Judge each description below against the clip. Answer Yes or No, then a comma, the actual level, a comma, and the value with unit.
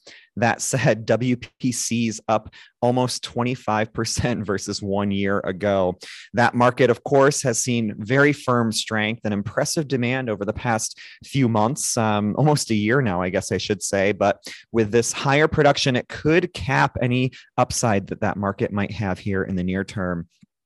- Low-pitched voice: Yes, low, 110 Hz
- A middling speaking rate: Yes, average, 165 wpm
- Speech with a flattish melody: No, average, 3.6 semitones